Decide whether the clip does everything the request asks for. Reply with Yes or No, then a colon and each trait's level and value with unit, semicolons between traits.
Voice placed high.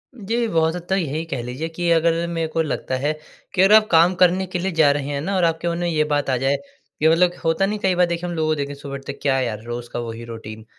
No: medium, 160 Hz